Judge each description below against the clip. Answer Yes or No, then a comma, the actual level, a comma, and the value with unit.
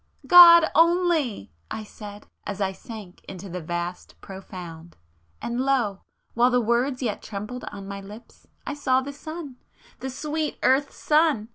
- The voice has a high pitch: Yes, high, 235 Hz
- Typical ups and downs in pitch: No, wide, 6.5 semitones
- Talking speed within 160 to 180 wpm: No, average, 145 wpm